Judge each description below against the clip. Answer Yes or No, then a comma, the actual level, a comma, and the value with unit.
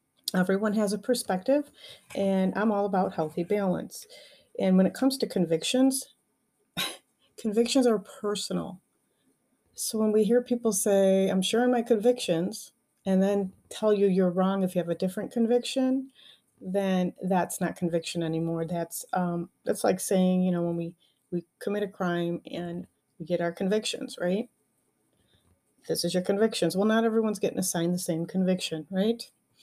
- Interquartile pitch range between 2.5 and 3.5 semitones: No, average, 4.0 semitones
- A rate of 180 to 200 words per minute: No, average, 160 wpm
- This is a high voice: Yes, high, 195 Hz